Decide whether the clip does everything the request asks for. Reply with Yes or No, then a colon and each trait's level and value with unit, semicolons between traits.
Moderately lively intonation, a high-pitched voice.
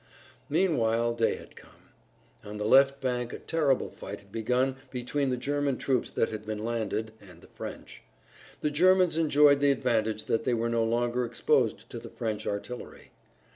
No: average, 3.7 semitones; low, 120 Hz